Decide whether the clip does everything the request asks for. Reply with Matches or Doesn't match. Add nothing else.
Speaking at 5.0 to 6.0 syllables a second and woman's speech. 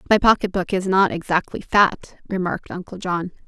Matches